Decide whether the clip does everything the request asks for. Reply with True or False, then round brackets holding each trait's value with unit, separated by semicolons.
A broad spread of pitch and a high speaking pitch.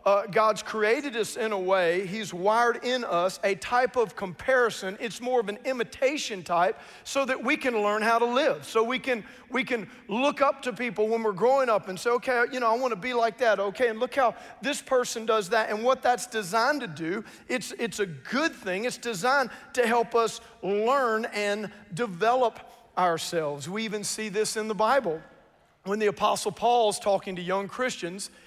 False (3.4 semitones; 225 Hz)